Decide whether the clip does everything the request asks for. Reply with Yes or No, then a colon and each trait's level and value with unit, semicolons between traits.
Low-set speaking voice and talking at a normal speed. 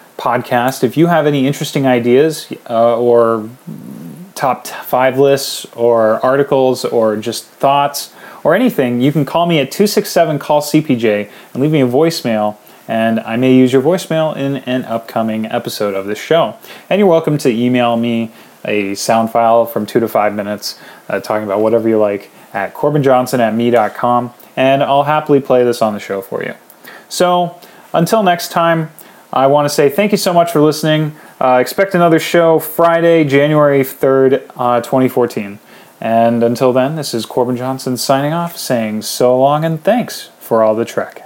Yes: low, 130 Hz; average, 175 wpm